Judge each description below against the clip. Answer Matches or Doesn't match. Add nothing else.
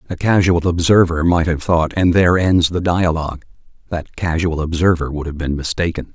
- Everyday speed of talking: Matches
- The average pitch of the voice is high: Doesn't match